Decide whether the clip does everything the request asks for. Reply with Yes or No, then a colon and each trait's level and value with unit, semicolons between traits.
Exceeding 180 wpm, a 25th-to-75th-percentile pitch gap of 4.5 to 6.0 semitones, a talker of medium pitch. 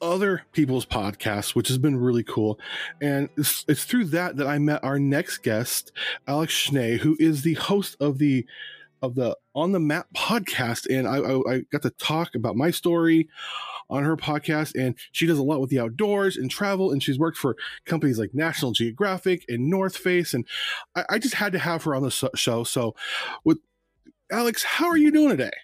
Yes: average, 200 wpm; wide, 5.5 semitones; medium, 150 Hz